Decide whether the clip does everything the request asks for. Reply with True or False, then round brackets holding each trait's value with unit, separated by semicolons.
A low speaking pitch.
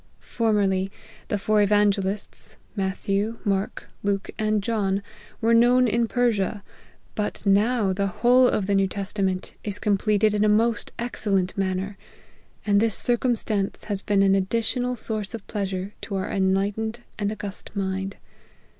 False (205 Hz)